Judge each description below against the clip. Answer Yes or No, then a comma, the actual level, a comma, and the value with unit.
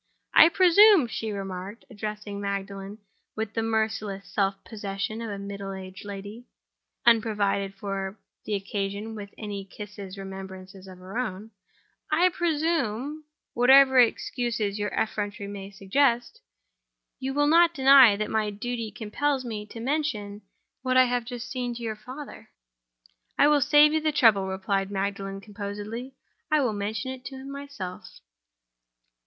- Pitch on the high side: Yes, high, 215 Hz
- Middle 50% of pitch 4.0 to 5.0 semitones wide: Yes, average, 4.5 semitones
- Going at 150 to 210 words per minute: No, average, 140 wpm